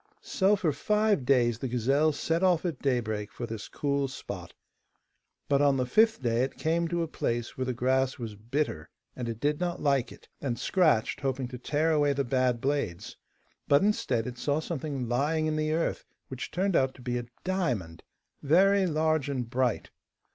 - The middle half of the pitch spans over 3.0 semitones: Yes, average, 4.4 semitones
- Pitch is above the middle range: No, medium, 140 Hz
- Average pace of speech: Yes, average, 190 wpm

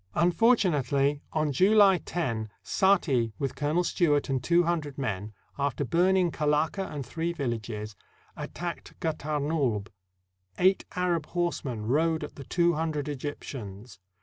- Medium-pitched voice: Yes, medium, 150 Hz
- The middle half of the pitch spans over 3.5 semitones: Yes, average, 4.8 semitones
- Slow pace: Yes, slow, 120 wpm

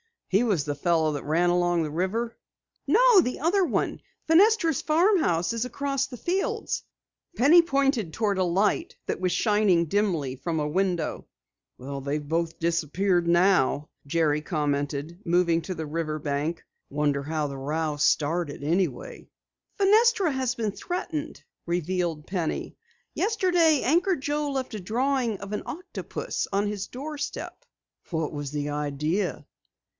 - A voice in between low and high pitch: Yes, medium, 180 Hz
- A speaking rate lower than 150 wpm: Yes, slow, 135 wpm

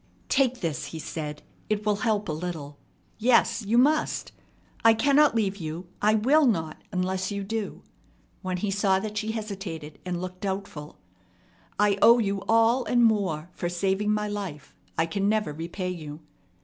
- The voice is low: No, high, 200 Hz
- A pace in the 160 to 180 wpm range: Yes, average, 165 wpm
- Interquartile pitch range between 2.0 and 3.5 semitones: No, average, 4.0 semitones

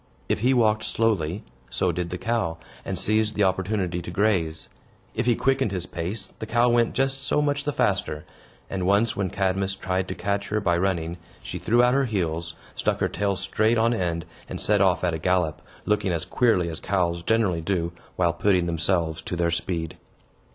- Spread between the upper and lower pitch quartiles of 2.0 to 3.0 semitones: No, average, 4.2 semitones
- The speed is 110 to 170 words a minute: No, average, 195 wpm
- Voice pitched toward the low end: Yes, very low, 95 Hz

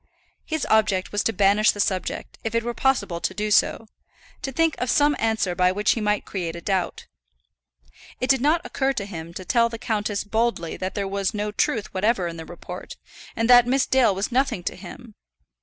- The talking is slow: No, fast, 205 wpm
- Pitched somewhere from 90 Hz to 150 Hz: No, high, 210 Hz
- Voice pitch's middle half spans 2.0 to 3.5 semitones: No, average, 4.0 semitones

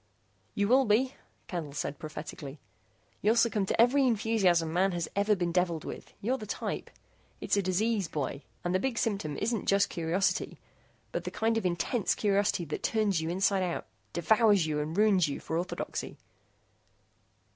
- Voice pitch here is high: Yes, high, 195 Hz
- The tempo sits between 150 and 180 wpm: Yes, average, 165 wpm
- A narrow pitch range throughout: No, average, 4.4 semitones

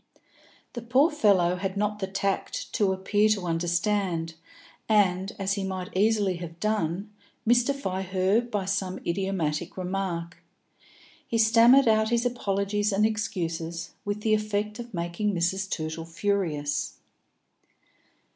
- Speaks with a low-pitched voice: No, high, 195 Hz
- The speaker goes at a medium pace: No, slow, 125 wpm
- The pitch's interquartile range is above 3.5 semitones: No, average, 3.2 semitones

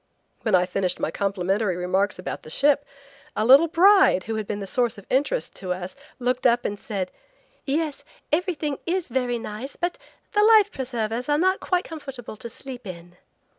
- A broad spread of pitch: Yes, wide, 6.9 semitones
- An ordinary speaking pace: Yes, average, 180 wpm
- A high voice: Yes, high, 245 Hz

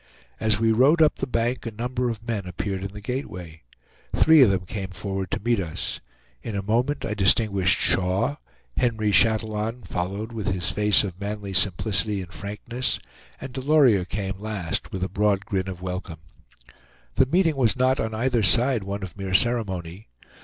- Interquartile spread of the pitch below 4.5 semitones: Yes, average, 3.7 semitones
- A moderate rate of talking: Yes, average, 175 wpm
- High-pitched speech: No, low, 105 Hz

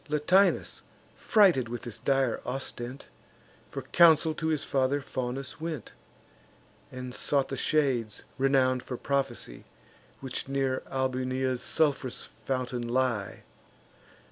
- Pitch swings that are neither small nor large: No, narrow, 2.0 semitones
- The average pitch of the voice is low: Yes, low, 130 Hz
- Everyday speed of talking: No, slow, 110 wpm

